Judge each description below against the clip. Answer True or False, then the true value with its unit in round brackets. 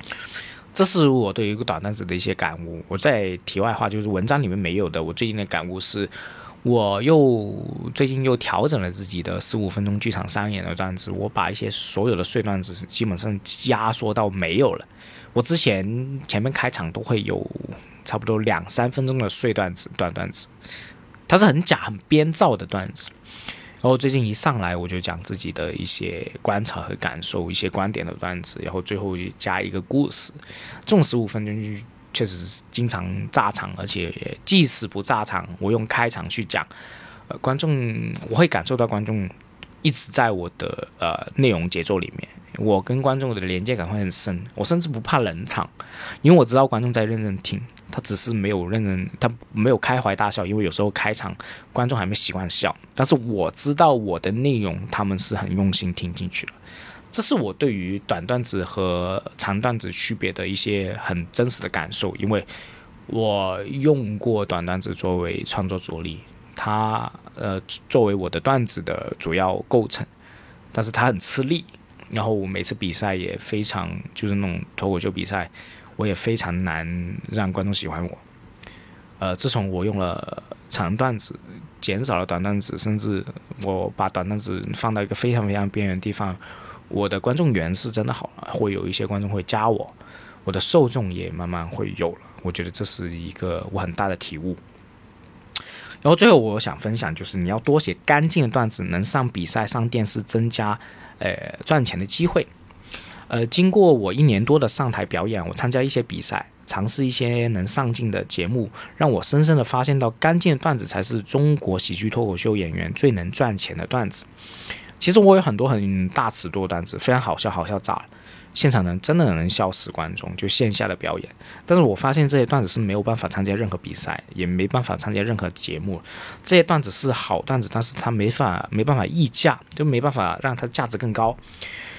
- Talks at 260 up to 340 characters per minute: True (285 characters per minute)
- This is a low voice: True (105 Hz)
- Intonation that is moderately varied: True (4.7 semitones)